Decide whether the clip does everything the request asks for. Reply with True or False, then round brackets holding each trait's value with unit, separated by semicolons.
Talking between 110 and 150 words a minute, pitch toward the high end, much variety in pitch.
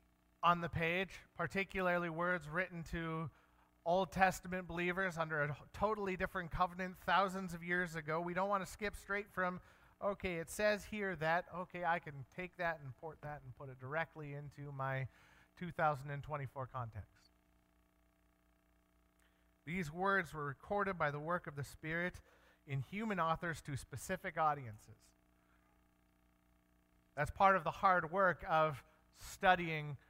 False (140 wpm; 160 Hz; 5.7 semitones)